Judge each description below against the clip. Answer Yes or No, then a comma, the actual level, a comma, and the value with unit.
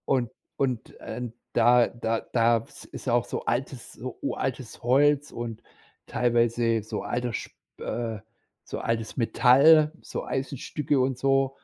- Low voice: Yes, low, 120 Hz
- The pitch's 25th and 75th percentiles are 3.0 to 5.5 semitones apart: No, narrow, 2.5 semitones